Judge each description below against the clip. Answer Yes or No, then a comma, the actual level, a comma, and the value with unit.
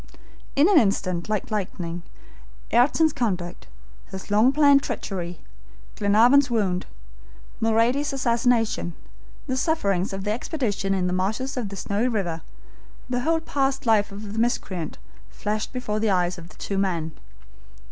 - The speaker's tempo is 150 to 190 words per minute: No, average, 140 wpm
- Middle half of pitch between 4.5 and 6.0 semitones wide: Yes, average, 4.8 semitones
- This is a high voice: Yes, high, 215 Hz